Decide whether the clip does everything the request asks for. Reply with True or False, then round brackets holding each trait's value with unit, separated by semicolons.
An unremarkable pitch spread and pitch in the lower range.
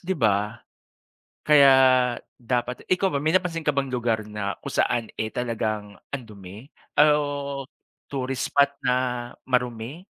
True (4.1 semitones; 125 Hz)